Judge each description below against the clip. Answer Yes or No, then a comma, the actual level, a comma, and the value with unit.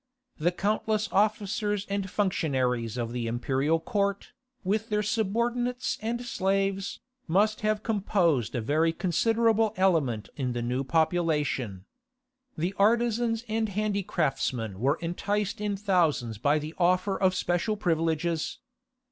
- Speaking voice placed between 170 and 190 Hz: Yes, medium, 185 Hz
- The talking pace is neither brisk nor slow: No, slow, 120 wpm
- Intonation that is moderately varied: No, wide, 5.9 semitones